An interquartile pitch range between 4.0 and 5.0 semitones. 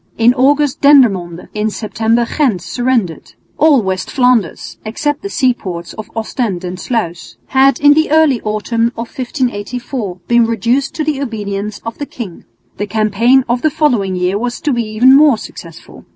Yes: average, 4.5 semitones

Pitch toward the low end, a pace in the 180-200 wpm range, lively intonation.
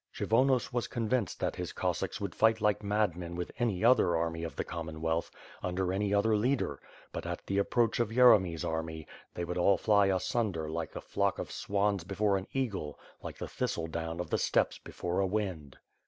No: very low, 95 Hz; average, 190 wpm; average, 4.4 semitones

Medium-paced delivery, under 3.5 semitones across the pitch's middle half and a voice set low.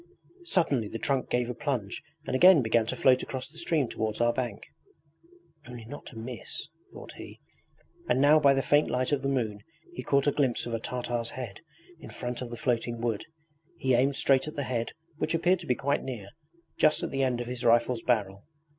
No: fast, 215 wpm; average, 2.9 semitones; low, 125 Hz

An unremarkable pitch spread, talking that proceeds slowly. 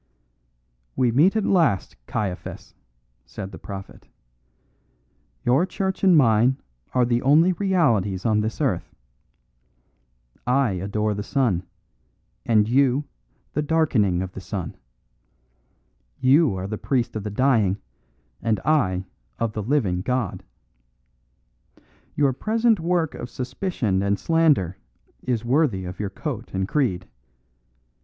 No: wide, 6.8 semitones; slow, 120 wpm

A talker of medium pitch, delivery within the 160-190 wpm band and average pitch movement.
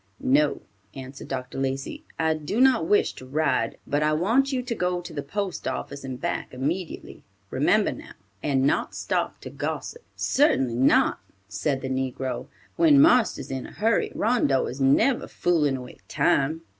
No: medium, 150 Hz; average, 165 wpm; wide, 8.0 semitones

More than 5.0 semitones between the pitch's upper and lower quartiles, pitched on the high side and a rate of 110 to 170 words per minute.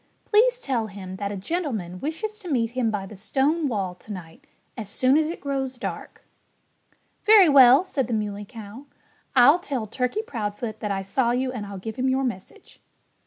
No: wide, 5.4 semitones; high, 245 Hz; average, 190 wpm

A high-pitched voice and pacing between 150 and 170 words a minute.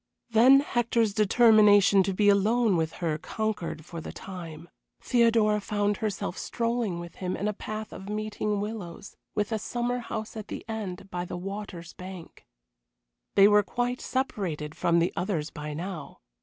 Yes: high, 205 Hz; average, 160 wpm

